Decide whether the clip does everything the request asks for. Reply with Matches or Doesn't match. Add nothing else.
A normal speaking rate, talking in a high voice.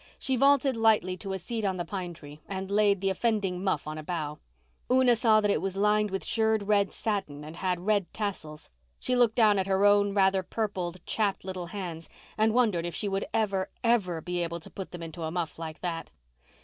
Doesn't match